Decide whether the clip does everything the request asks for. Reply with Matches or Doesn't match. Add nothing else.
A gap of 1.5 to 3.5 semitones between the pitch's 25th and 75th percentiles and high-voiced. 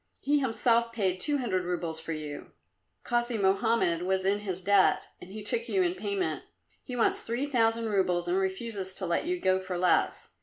Doesn't match